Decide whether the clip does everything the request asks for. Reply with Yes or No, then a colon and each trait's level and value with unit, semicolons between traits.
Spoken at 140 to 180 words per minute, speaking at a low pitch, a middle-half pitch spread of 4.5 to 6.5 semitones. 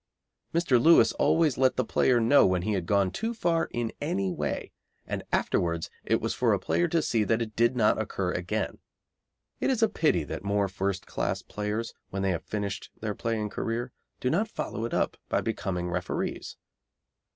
No: average, 190 wpm; low, 110 Hz; wide, 5.5 semitones